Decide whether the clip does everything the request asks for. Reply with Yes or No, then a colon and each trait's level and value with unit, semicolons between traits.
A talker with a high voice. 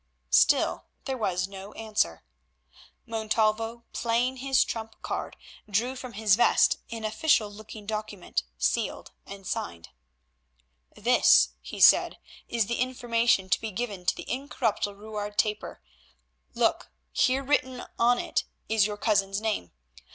Yes: high, 220 Hz